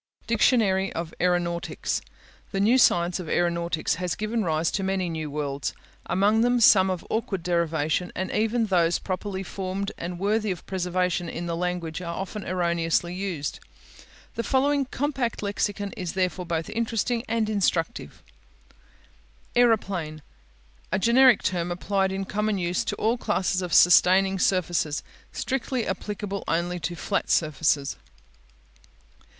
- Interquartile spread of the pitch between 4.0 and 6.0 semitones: No, average, 3.5 semitones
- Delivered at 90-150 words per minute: Yes, slow, 135 wpm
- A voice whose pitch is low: No, medium, 185 Hz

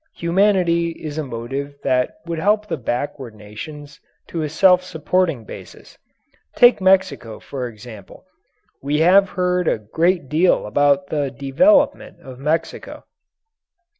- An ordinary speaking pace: No, slow, 130 wpm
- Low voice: No, medium, 155 Hz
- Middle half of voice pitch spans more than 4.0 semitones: Yes, wide, 5.4 semitones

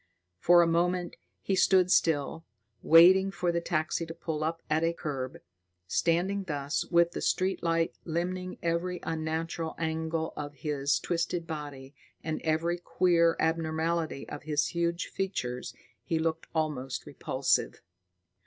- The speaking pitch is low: No, medium, 165 Hz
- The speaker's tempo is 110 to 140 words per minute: Yes, slow, 135 wpm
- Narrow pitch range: Yes, narrow, 1.7 semitones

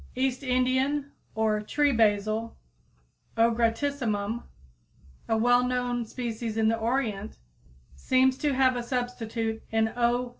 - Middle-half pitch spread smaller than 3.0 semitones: Yes, narrow, 2.5 semitones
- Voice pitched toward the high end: Yes, high, 240 Hz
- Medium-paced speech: No, slow, 125 wpm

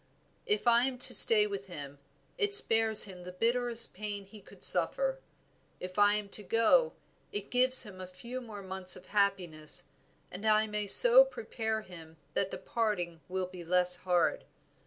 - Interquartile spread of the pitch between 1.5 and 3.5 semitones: No, average, 4.5 semitones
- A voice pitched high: Yes, high, 210 Hz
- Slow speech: No, average, 175 wpm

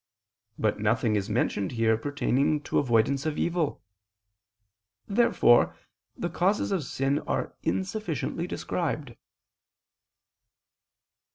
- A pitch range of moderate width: No, wide, 7.1 semitones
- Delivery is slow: Yes, slow, 95 wpm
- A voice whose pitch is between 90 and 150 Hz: Yes, medium, 140 Hz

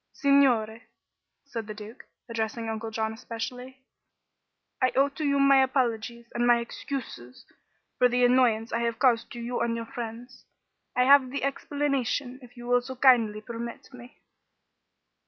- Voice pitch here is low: No, high, 245 Hz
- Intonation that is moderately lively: No, narrow, 2.3 semitones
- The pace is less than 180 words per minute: Yes, average, 155 wpm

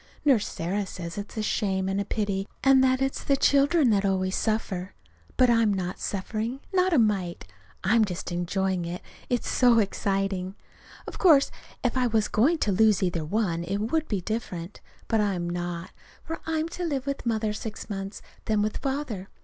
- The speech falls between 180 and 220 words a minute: Yes, average, 185 wpm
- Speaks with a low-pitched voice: No, high, 210 Hz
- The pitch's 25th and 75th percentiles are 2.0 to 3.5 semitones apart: No, average, 4.7 semitones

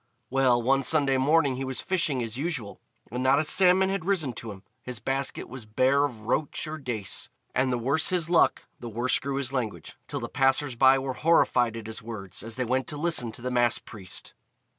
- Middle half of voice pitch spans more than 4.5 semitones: No, average, 3.4 semitones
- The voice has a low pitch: Yes, low, 130 Hz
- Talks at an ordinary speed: No, fast, 215 wpm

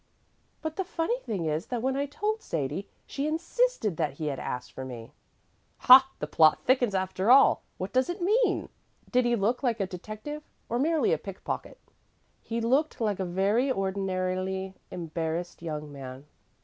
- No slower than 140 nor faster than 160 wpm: No, average, 170 wpm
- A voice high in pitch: Yes, high, 205 Hz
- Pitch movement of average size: No, wide, 7.5 semitones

